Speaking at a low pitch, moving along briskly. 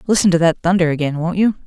No: medium, 175 Hz; fast, 250 wpm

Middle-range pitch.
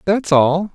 Yes: medium, 175 Hz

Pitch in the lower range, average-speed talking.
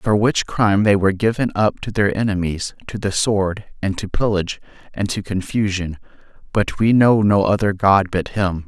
Yes: low, 100 Hz; average, 185 wpm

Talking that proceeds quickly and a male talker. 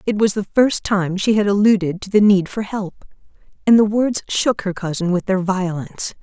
No: fast, 210 wpm; female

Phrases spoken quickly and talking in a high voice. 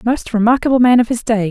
Yes: fast, 240 wpm; high, 235 Hz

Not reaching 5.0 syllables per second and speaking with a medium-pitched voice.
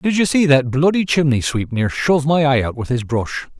No: 5.3 syllables/s; medium, 145 Hz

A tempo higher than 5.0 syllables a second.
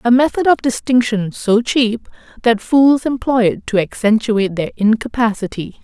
No: 4.8 syllables/s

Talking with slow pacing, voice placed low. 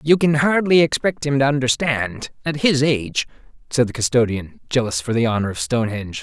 No: average, 175 wpm; low, 130 Hz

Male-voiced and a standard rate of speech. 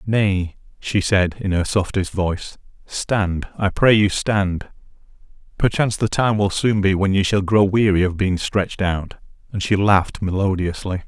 Yes: male; average, 170 wpm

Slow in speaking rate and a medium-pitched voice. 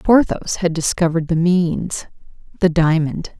Yes: slow, 125 wpm; medium, 170 Hz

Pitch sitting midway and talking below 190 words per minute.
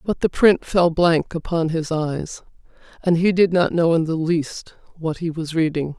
No: medium, 165 Hz; average, 200 wpm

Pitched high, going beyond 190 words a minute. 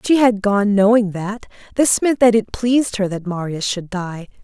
Yes: high, 210 Hz; fast, 205 wpm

